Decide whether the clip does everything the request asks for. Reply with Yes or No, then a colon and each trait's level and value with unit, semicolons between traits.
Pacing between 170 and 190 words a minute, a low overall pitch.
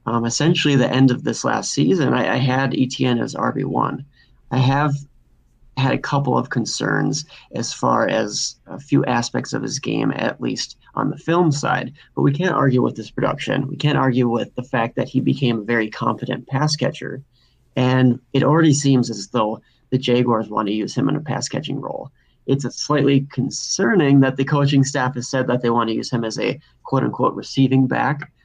No: average, 200 wpm; low, 130 Hz